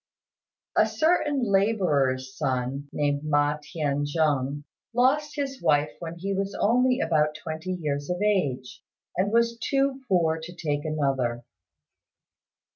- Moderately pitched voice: Yes, medium, 160 Hz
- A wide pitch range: Yes, wide, 6.3 semitones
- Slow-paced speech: Yes, slow, 125 wpm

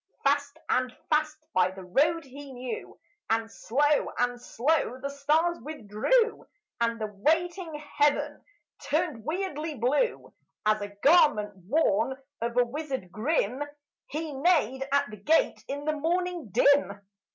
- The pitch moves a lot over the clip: No, average, 5.0 semitones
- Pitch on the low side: No, very high, 280 Hz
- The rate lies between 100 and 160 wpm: Yes, slow, 135 wpm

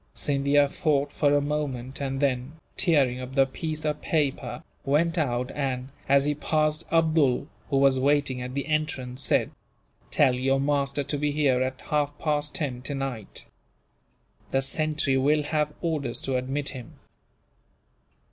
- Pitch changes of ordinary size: No, narrow, 2.2 semitones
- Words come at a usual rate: Yes, average, 150 wpm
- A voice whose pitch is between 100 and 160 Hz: Yes, medium, 140 Hz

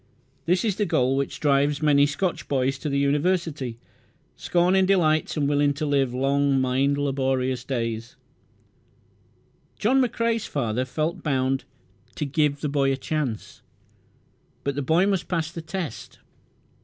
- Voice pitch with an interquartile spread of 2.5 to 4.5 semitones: Yes, average, 3.6 semitones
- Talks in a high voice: No, medium, 145 Hz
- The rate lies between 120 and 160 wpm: Yes, average, 145 wpm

